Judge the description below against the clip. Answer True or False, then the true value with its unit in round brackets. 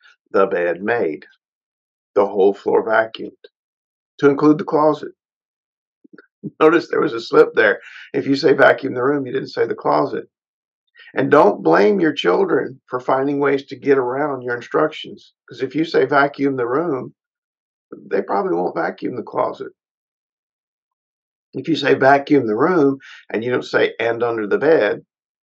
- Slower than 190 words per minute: True (160 wpm)